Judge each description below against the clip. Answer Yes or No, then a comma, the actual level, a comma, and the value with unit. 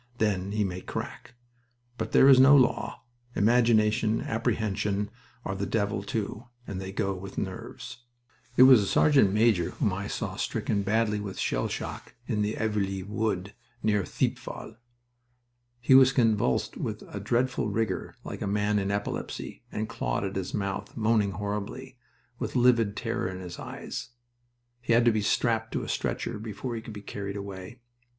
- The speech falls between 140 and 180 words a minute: Yes, average, 165 wpm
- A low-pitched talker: Yes, low, 105 Hz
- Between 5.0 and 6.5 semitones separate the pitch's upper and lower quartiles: No, average, 2.8 semitones